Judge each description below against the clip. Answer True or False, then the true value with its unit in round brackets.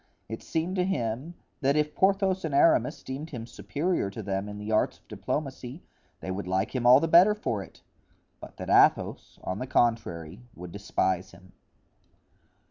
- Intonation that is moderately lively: False (8.1 semitones)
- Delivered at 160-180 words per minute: True (175 wpm)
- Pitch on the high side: False (120 Hz)